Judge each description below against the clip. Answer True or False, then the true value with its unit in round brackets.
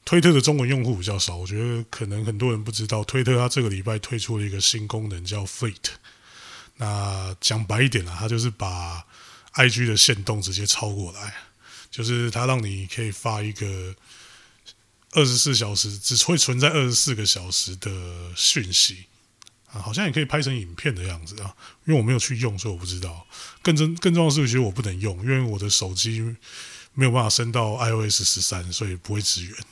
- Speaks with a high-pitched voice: False (110 Hz)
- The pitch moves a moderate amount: True (3.7 semitones)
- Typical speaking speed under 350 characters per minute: True (310 characters per minute)